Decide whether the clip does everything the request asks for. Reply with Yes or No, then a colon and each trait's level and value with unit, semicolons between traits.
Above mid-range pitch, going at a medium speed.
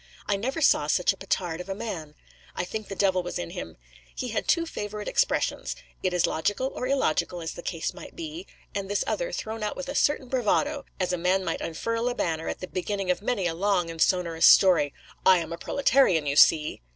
No: high, 195 Hz; fast, 225 wpm